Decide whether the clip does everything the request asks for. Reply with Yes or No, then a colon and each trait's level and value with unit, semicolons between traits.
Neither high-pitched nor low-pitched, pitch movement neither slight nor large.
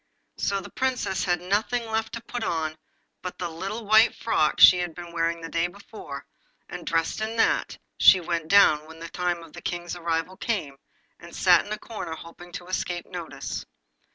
Yes: medium, 175 Hz; average, 3.8 semitones